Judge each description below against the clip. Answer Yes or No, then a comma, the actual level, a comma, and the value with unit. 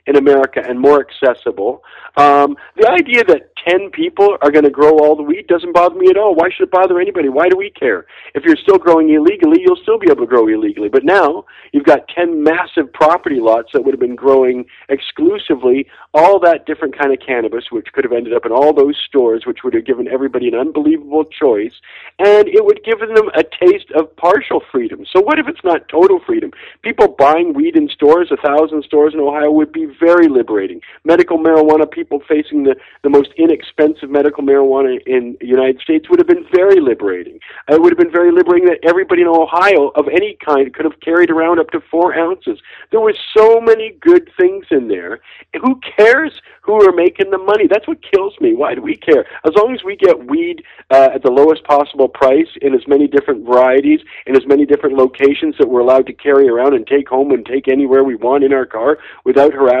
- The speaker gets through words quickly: Yes, fast, 215 wpm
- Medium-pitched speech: Yes, medium, 180 Hz